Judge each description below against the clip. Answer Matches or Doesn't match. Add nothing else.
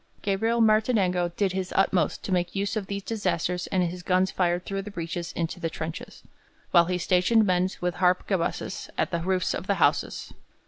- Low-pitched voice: Doesn't match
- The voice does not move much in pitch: Matches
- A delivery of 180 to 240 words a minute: Matches